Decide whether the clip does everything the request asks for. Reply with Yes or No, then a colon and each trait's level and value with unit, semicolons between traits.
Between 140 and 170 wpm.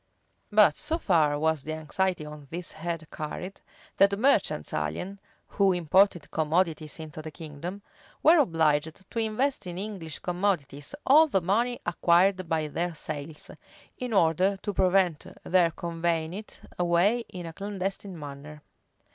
Yes: average, 145 wpm